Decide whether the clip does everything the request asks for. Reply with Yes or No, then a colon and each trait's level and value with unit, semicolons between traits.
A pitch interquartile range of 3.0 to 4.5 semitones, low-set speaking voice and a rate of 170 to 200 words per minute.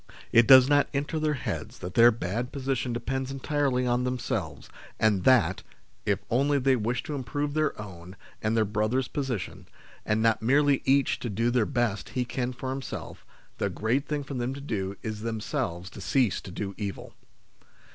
Yes: average, 4.0 semitones; low, 125 Hz; average, 180 wpm